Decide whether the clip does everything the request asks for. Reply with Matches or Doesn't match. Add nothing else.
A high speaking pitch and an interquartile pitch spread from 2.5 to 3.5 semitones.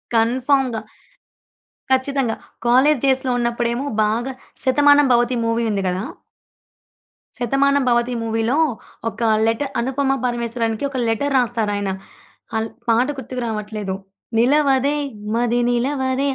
Matches